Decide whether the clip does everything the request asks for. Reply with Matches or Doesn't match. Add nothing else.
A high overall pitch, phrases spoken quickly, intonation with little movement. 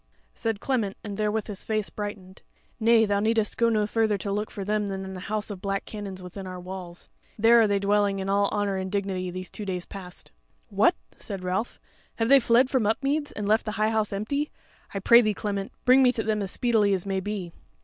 Matches